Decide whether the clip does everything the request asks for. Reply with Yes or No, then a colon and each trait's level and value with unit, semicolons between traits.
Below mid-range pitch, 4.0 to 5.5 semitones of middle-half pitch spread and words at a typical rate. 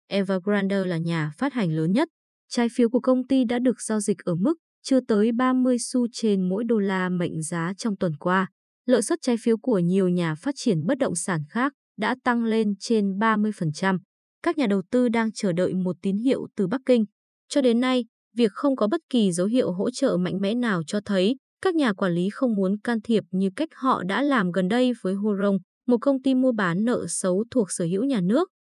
No: high, 220 Hz; average, 4.9 semitones; average, 225 wpm